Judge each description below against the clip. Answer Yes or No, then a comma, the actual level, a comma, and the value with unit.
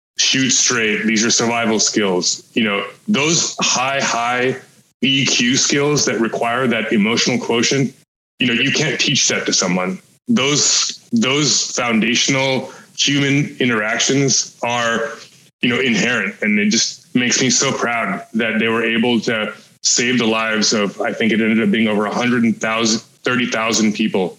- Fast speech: No, average, 160 wpm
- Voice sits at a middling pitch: No, low, 115 Hz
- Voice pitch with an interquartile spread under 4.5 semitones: Yes, average, 3.2 semitones